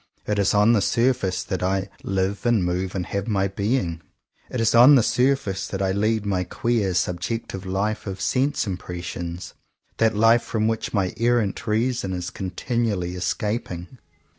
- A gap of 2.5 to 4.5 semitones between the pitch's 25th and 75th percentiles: Yes, average, 3.7 semitones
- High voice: No, low, 100 Hz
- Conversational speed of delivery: Yes, average, 170 wpm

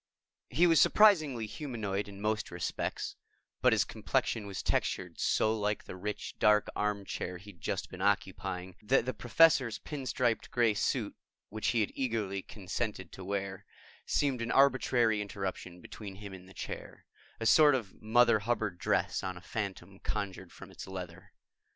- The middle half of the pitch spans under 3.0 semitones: No, average, 3.9 semitones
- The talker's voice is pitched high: No, low, 105 Hz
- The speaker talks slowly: No, average, 160 wpm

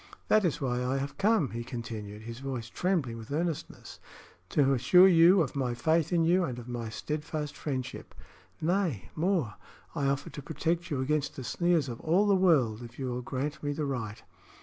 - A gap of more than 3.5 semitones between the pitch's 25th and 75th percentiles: Yes, average, 5.2 semitones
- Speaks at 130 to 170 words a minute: No, average, 195 wpm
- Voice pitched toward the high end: No, medium, 140 Hz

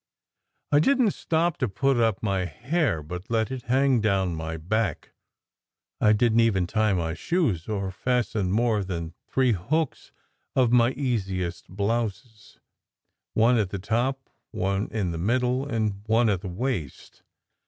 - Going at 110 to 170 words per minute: Yes, average, 155 wpm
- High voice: No, low, 110 Hz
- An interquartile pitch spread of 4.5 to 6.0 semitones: Yes, average, 4.8 semitones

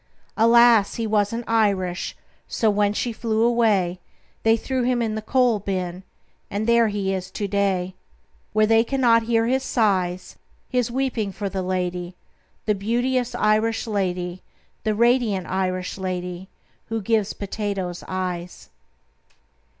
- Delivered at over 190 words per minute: No, slow, 135 wpm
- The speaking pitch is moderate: No, high, 210 Hz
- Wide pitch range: No, average, 3.5 semitones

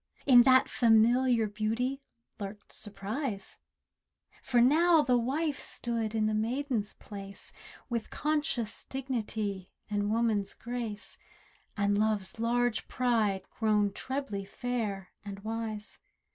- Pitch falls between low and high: No, high, 225 Hz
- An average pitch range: Yes, average, 3.3 semitones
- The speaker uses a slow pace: Yes, slow, 110 wpm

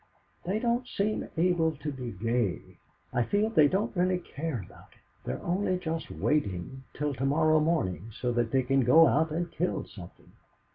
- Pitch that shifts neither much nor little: No, wide, 6.5 semitones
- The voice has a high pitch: No, medium, 155 Hz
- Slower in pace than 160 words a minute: No, average, 180 wpm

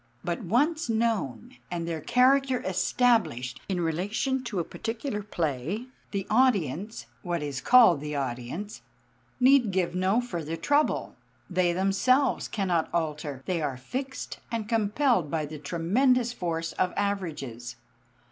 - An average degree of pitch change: No, wide, 6.8 semitones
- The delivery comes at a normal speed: No, slow, 130 wpm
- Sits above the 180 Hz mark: Yes, high, 190 Hz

